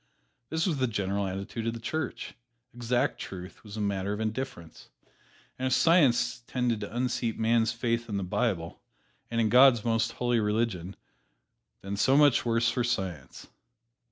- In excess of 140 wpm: Yes, average, 165 wpm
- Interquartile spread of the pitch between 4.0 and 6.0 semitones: No, average, 3.3 semitones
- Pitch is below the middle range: Yes, low, 115 Hz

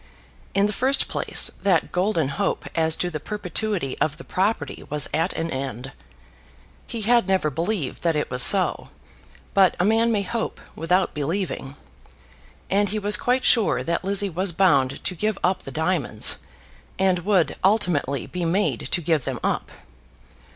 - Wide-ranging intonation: No, average, 4.6 semitones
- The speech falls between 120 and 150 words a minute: No, average, 165 wpm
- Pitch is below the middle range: No, medium, 180 Hz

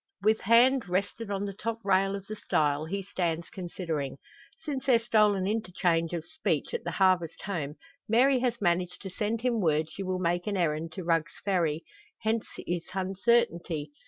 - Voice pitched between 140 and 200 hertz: Yes, high, 190 Hz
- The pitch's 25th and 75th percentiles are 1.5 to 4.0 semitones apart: No, average, 4.5 semitones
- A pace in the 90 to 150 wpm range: No, average, 175 wpm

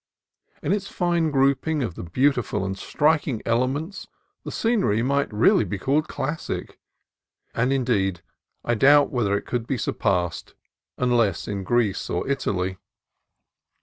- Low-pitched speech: Yes, low, 125 Hz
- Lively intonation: Yes, wide, 6.1 semitones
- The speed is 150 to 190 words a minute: No, slow, 135 wpm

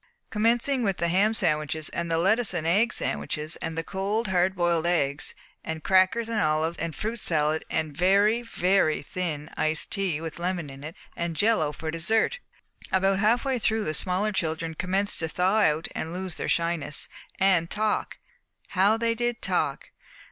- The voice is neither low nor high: Yes, medium, 180 Hz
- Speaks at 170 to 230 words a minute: Yes, average, 175 wpm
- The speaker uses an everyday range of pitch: Yes, average, 4.7 semitones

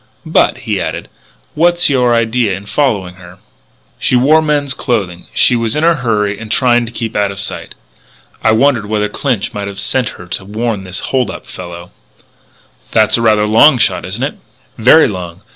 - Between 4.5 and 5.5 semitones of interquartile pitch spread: No, average, 4.1 semitones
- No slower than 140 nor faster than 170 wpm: No, average, 185 wpm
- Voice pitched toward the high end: No, low, 110 Hz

